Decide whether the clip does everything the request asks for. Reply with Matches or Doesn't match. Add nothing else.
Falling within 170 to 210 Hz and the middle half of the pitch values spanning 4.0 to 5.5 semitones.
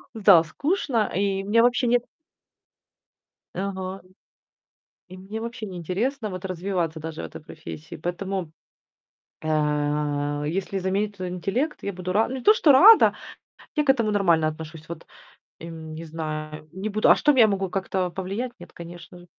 Matches